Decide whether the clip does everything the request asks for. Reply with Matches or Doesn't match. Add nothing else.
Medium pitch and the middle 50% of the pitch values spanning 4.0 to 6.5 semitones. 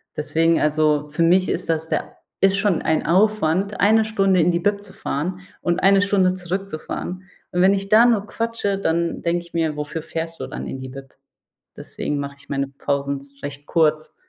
Matches